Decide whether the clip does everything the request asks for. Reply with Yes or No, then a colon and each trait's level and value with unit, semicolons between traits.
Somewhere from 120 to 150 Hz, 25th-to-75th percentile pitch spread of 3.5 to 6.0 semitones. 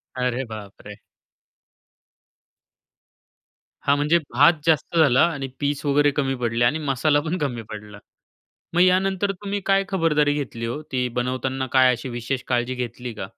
Yes: low, 135 Hz; average, 4.0 semitones